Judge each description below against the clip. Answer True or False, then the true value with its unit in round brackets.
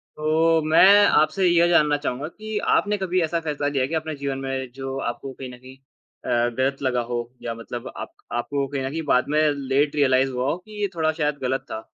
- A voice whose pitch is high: False (145 Hz)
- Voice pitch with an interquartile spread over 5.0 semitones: False (3.3 semitones)